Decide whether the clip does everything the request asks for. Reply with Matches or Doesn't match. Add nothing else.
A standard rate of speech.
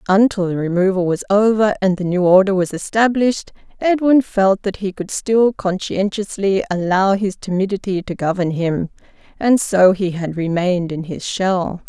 Matches